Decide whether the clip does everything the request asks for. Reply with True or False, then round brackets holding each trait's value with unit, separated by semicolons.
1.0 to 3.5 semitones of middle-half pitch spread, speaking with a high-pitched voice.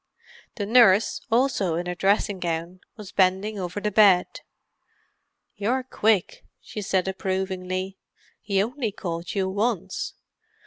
True (2.4 semitones; 195 Hz)